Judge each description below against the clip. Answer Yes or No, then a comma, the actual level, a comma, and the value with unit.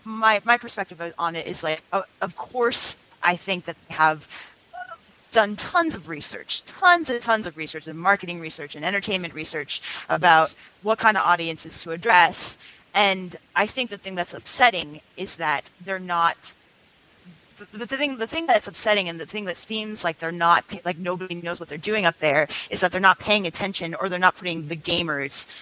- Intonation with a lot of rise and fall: No, average, 4.1 semitones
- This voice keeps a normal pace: Yes, average, 190 wpm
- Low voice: No, medium, 180 Hz